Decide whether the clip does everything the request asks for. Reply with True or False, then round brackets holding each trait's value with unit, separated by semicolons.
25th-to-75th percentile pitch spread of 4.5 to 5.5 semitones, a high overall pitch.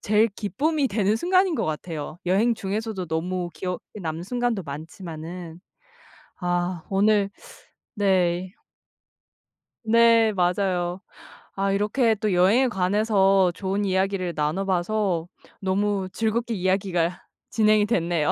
False (3.4 semitones; 195 Hz)